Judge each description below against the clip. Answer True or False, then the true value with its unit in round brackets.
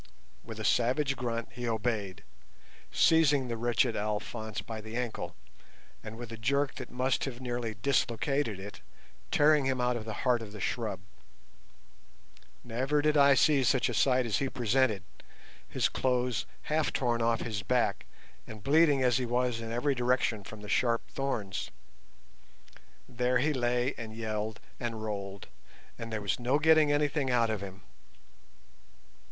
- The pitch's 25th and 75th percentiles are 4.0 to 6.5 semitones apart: False (3.2 semitones)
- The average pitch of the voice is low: True (120 Hz)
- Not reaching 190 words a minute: True (160 wpm)